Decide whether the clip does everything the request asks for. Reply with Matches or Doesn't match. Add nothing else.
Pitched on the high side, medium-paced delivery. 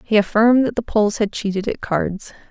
Doesn't match